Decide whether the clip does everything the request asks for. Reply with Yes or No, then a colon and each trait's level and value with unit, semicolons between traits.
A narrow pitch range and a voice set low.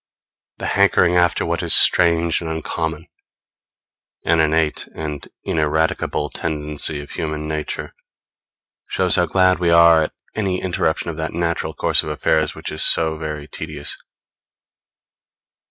Yes: narrow, 1.6 semitones; very low, 80 Hz